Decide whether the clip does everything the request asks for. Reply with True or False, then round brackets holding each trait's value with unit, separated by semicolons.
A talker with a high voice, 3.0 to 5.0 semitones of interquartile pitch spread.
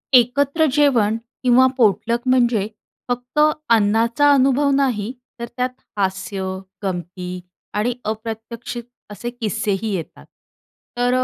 True (230 Hz; 3.4 semitones)